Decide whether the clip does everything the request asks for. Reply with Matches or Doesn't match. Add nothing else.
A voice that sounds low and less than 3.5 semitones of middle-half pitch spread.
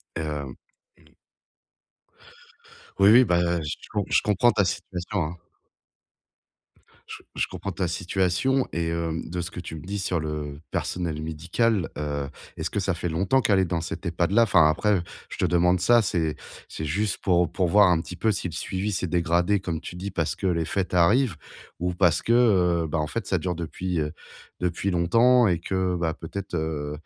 Matches